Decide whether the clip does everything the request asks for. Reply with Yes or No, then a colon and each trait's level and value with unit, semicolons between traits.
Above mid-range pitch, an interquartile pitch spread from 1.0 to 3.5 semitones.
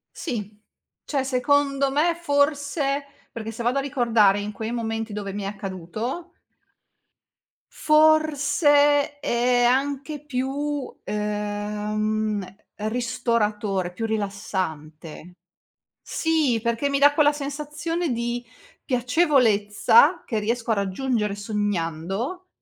No: high, 235 Hz; wide, 5.5 semitones